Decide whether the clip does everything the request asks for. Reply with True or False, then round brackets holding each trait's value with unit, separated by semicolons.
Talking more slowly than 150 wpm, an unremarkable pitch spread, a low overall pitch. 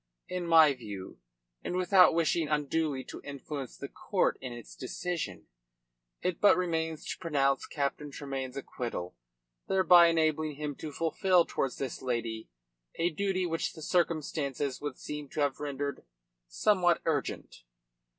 False (140 wpm; 3.7 semitones; 150 Hz)